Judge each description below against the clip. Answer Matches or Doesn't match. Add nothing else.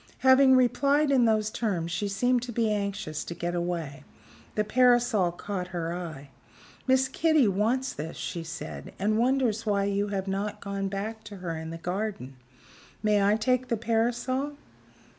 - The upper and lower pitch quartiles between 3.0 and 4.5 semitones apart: Doesn't match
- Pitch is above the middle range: Matches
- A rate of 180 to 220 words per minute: Doesn't match